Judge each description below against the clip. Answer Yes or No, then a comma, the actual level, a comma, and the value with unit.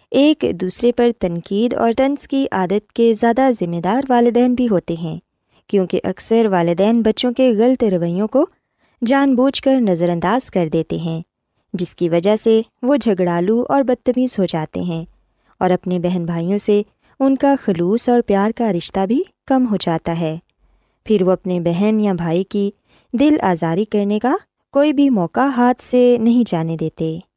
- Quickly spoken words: No, average, 175 wpm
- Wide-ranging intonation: Yes, wide, 5.7 semitones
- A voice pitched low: No, high, 210 Hz